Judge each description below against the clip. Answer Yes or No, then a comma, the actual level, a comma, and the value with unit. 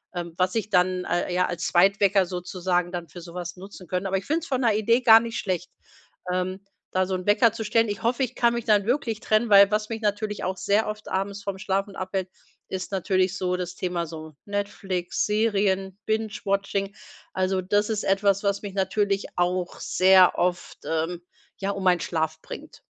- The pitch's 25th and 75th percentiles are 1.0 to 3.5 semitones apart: Yes, narrow, 2.4 semitones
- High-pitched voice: Yes, high, 195 Hz